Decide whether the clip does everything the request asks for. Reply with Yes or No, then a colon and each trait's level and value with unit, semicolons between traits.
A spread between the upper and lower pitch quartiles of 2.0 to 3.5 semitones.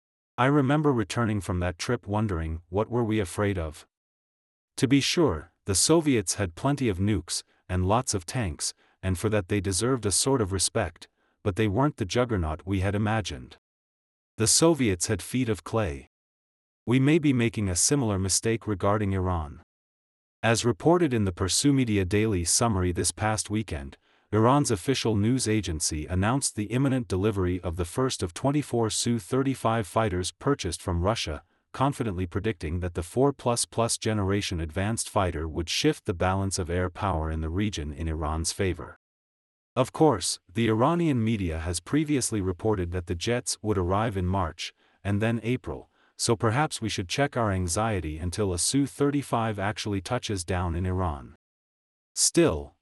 No: average, 4.6 semitones